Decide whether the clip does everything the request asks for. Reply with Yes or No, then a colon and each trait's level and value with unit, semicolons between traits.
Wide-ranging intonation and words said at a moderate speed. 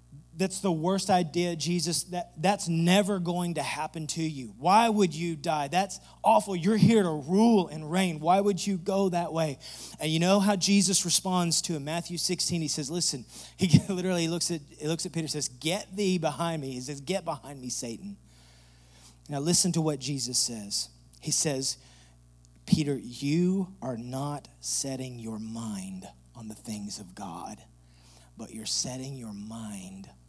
Yes: wide, 7.4 semitones; average, 175 wpm